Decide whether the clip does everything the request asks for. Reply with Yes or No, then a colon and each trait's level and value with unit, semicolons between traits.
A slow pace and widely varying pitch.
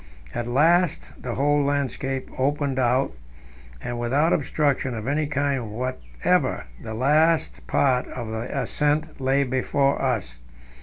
No: slow, 125 wpm; average, 3.2 semitones